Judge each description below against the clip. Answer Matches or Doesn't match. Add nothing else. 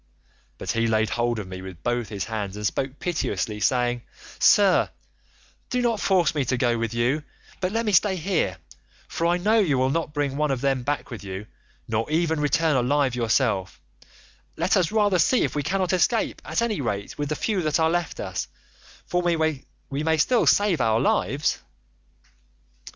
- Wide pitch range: Matches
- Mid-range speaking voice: Matches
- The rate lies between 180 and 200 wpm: Matches